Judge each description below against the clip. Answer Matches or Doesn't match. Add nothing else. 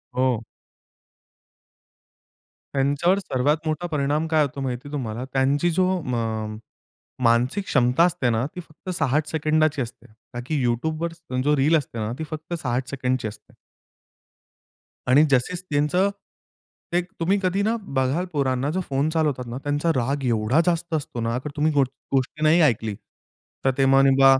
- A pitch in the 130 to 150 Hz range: Matches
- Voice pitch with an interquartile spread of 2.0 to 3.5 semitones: Doesn't match